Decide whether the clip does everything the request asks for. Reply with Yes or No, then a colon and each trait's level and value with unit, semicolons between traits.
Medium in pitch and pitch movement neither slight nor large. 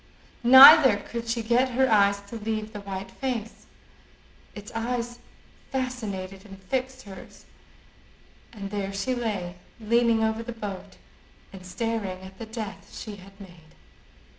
No: high, 215 Hz; average, 3.2 semitones